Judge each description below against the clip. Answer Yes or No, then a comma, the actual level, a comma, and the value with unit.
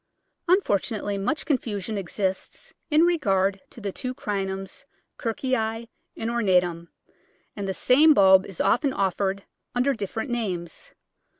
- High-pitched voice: Yes, high, 205 Hz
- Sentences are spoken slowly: Yes, slow, 120 wpm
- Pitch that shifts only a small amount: No, average, 4.6 semitones